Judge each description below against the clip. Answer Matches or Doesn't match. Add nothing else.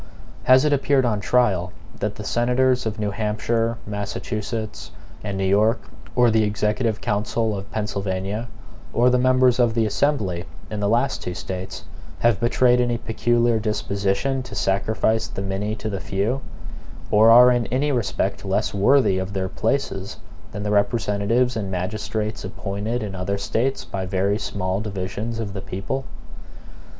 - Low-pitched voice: Matches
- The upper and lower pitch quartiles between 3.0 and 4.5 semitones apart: Matches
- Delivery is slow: Doesn't match